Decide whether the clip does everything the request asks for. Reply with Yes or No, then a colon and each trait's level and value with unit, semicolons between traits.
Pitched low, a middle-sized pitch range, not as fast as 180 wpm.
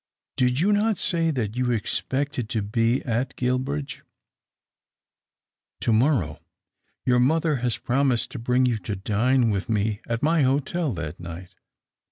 Yes: low, 125 Hz; average, 4.2 semitones; average, 155 wpm